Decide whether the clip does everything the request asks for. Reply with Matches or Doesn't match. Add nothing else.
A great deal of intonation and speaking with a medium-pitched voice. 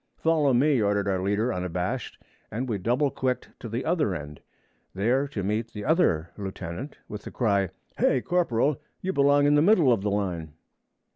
Doesn't match